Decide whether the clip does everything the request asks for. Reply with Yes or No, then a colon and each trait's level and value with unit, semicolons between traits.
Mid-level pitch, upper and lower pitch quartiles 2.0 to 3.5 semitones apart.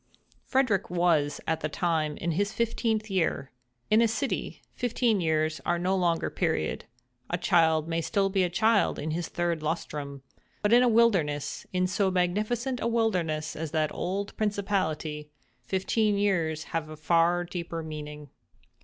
No: medium, 175 Hz; average, 4.7 semitones